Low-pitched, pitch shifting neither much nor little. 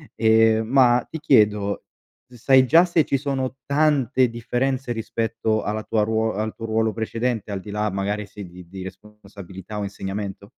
Yes: low, 110 Hz; average, 3.4 semitones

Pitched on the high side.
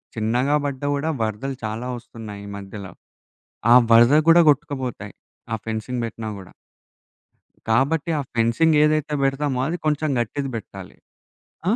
No: low, 125 Hz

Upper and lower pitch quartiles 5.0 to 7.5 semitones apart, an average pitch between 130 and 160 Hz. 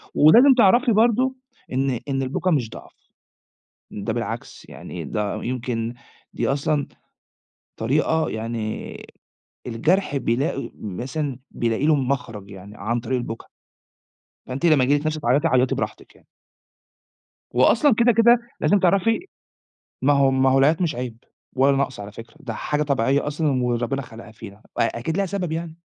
Yes: average, 5.3 semitones; low, 135 Hz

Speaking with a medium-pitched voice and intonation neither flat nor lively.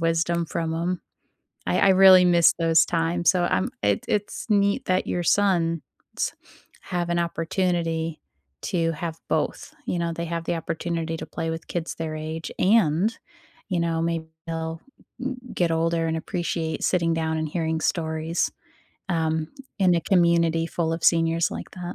No: medium, 165 Hz; narrow, 1.2 semitones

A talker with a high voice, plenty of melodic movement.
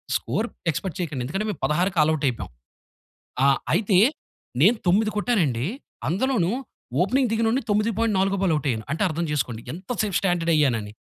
No: medium, 180 Hz; wide, 5.8 semitones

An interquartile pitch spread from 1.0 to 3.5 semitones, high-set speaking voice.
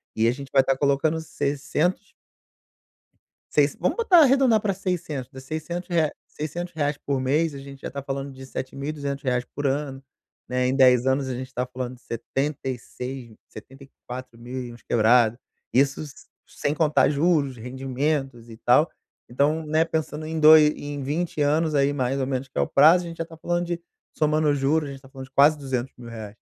No: average, 3.1 semitones; medium, 140 Hz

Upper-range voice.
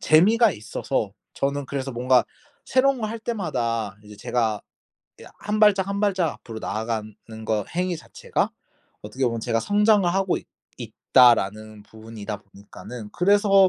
No: low, 130 Hz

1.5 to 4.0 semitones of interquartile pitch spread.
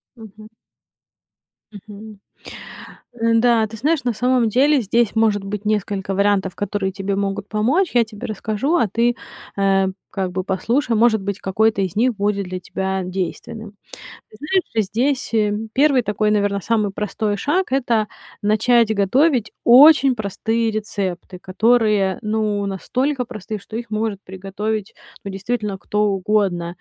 Yes: average, 3.0 semitones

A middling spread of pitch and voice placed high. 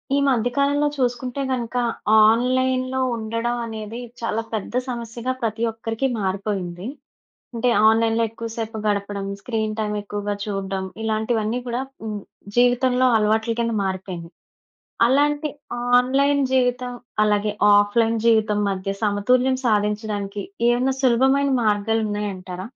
Yes: average, 3.1 semitones; high, 225 Hz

